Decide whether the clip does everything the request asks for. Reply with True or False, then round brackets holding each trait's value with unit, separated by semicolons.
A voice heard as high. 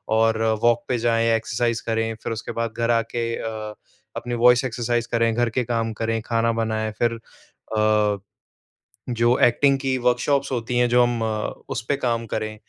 False (115 Hz)